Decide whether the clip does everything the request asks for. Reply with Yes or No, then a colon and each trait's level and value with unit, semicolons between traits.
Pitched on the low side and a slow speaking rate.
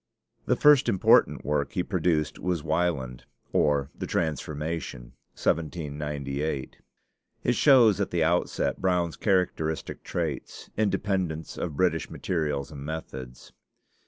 Yes: very low, 80 Hz; slow, 110 wpm